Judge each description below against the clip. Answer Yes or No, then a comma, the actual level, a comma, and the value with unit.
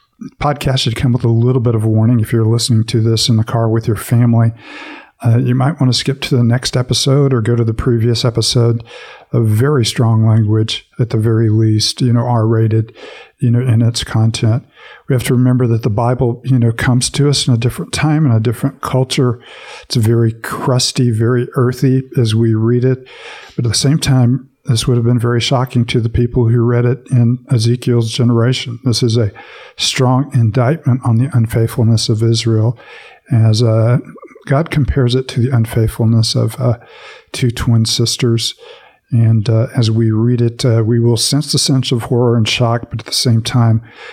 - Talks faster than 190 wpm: Yes, average, 200 wpm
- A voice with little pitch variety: Yes, narrow, 1.9 semitones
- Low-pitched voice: Yes, low, 120 Hz